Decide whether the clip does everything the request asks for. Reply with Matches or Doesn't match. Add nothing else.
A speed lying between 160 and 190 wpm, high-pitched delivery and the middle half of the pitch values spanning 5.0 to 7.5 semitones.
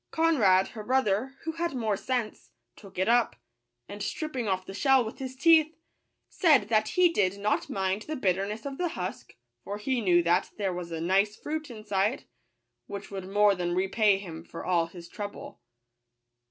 Matches